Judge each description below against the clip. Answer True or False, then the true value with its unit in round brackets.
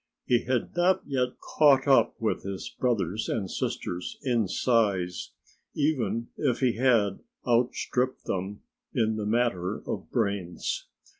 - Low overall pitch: True (115 Hz)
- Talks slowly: True (130 wpm)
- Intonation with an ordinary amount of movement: True (4.3 semitones)